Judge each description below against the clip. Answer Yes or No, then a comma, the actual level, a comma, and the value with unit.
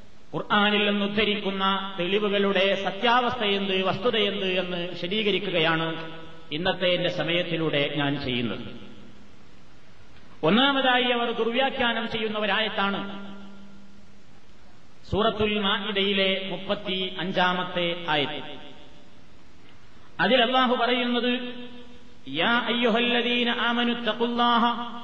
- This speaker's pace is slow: Yes, slow, 55 wpm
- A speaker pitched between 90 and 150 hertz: No, high, 200 Hz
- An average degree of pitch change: Yes, average, 5.0 semitones